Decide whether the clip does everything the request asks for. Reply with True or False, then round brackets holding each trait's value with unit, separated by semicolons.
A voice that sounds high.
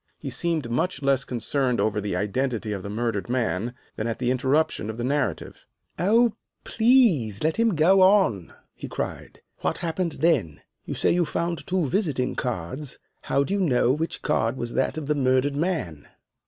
False (135 Hz)